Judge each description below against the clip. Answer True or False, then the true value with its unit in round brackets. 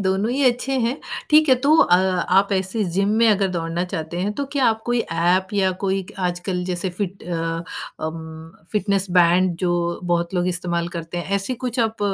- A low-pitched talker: False (185 Hz)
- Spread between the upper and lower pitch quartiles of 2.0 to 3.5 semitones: True (3.2 semitones)